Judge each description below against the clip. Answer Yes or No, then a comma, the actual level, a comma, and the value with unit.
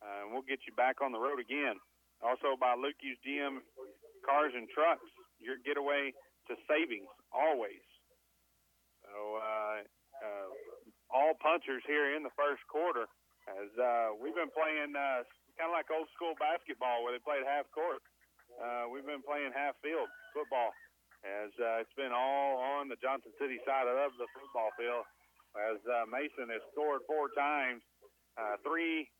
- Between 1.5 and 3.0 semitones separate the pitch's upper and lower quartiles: No, average, 3.9 semitones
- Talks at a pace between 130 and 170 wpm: Yes, average, 160 wpm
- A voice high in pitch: No, low, 135 Hz